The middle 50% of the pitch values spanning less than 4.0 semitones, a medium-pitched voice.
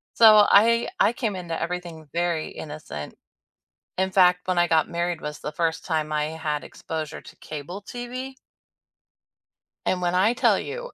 No: average, 4.3 semitones; medium, 175 Hz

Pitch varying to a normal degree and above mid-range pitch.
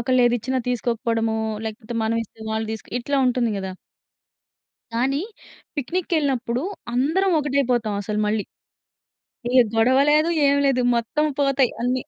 Yes: average, 3.5 semitones; high, 245 Hz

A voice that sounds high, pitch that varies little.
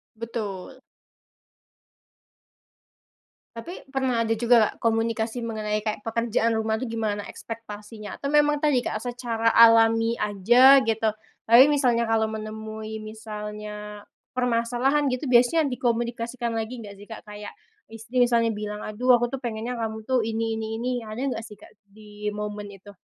Yes: high, 225 Hz; narrow, 2.0 semitones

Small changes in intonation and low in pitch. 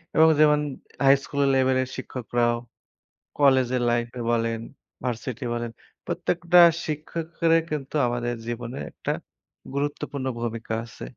No: average, 3.6 semitones; low, 130 Hz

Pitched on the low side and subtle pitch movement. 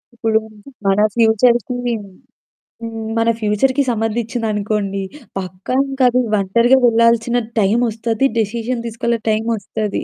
No: high, 225 Hz; narrow, 2.2 semitones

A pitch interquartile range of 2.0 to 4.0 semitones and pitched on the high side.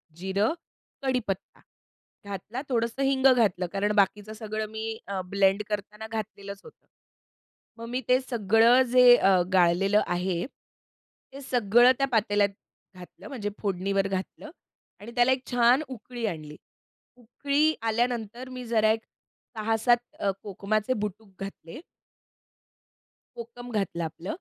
Yes: average, 3.6 semitones; high, 220 Hz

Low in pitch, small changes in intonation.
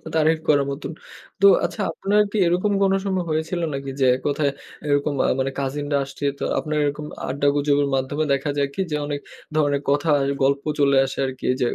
No: medium, 145 Hz; narrow, 2.0 semitones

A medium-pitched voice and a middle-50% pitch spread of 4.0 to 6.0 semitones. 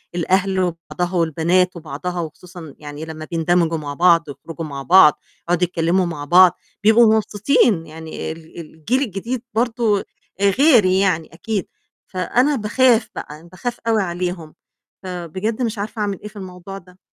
Yes: medium, 180 Hz; average, 4.3 semitones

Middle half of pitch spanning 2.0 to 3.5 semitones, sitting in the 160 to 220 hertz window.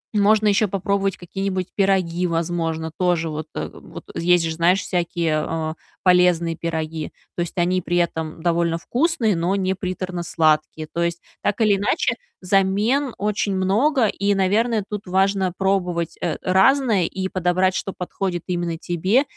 Yes: average, 2.7 semitones; medium, 185 Hz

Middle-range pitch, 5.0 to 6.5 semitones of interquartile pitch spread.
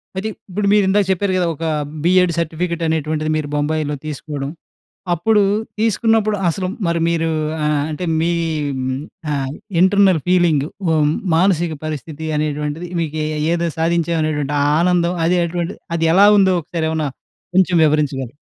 No: medium, 165 Hz; average, 3.0 semitones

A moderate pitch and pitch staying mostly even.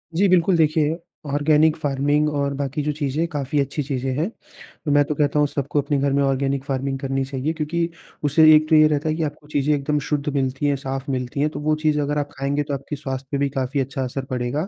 Yes: medium, 145 Hz; narrow, 1.8 semitones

